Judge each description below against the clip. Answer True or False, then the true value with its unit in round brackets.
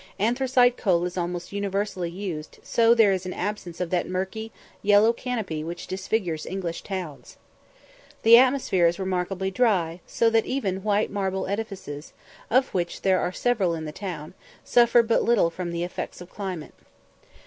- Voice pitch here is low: False (190 Hz)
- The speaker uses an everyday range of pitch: True (4.0 semitones)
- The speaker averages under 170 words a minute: True (160 wpm)